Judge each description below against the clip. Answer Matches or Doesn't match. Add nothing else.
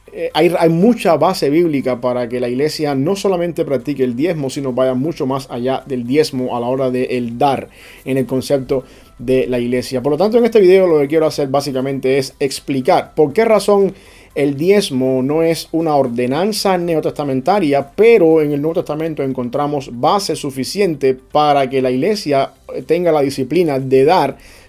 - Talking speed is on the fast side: Doesn't match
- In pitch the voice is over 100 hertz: Matches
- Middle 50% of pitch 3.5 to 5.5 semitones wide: Matches